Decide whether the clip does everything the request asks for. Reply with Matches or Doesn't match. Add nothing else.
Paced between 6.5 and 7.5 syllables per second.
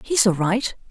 Doesn't match